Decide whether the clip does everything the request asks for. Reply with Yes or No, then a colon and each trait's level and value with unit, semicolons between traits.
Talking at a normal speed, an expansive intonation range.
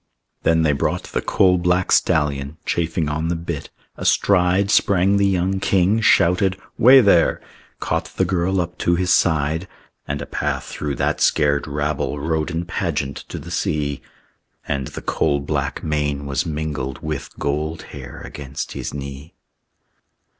No: average, 155 wpm; average, 3.9 semitones